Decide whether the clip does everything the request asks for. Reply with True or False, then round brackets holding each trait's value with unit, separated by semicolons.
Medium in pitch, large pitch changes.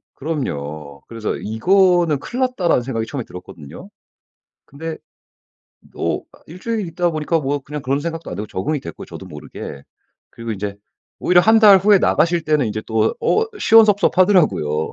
True (155 Hz; 8.6 semitones)